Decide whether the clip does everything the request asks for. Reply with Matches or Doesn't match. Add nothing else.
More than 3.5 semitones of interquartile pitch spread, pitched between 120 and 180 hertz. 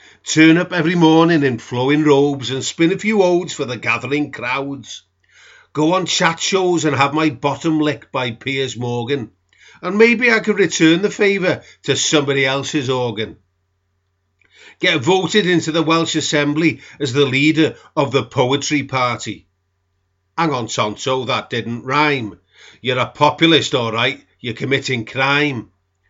Matches